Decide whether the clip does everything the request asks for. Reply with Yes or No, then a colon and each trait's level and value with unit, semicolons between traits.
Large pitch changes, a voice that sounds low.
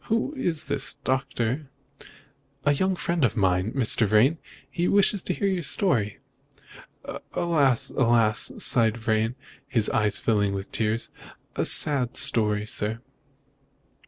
Yes: wide, 6.1 semitones; low, 120 Hz